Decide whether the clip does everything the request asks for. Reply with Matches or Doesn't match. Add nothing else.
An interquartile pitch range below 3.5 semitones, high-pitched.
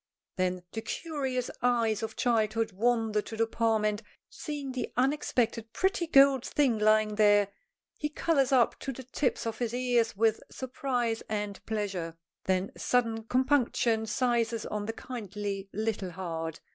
Matches